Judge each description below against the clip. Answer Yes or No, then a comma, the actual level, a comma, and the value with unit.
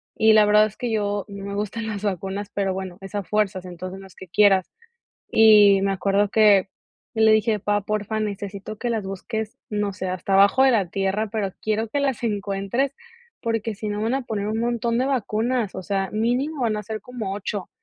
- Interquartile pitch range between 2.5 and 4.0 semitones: No, narrow, 2.1 semitones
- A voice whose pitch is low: No, high, 210 Hz